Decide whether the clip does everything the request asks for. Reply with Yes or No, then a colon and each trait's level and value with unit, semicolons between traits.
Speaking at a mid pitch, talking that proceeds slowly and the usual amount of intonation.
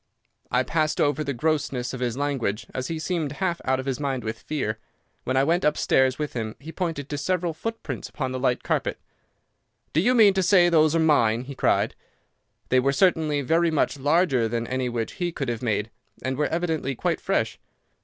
No: medium, 145 Hz; average, 200 wpm; average, 4.3 semitones